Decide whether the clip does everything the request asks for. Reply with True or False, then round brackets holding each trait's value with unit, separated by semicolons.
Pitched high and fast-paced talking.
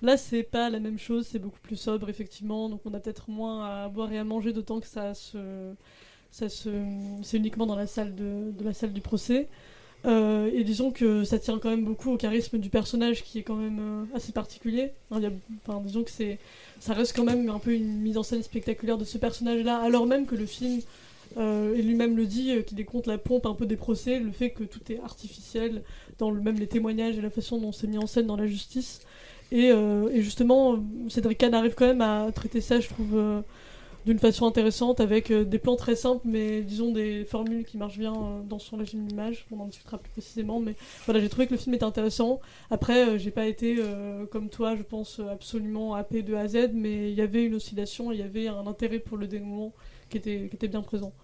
True (220 Hz; 240 wpm)